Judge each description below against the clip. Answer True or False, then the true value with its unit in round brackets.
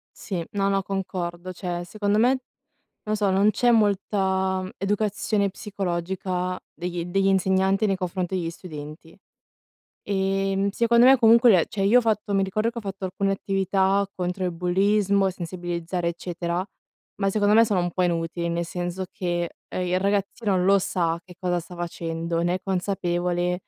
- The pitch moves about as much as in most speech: False (2.2 semitones)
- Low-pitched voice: False (190 Hz)